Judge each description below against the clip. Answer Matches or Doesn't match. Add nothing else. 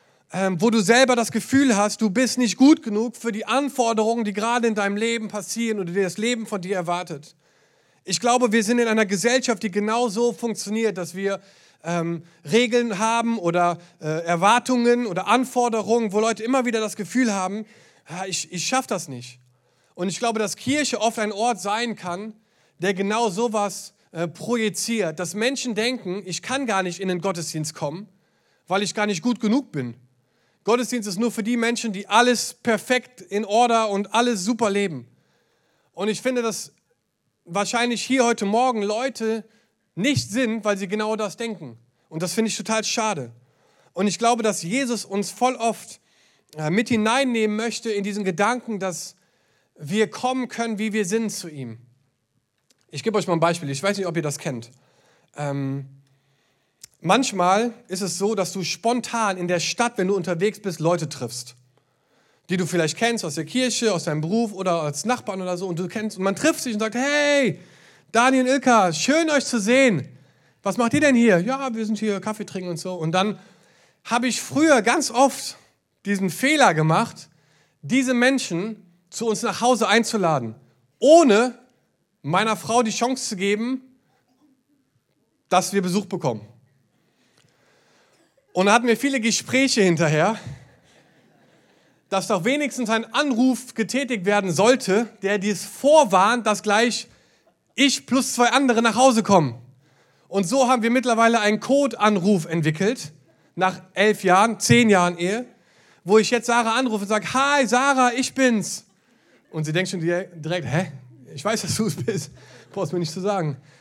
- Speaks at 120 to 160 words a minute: Doesn't match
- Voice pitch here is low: Doesn't match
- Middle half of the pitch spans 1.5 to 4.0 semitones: Doesn't match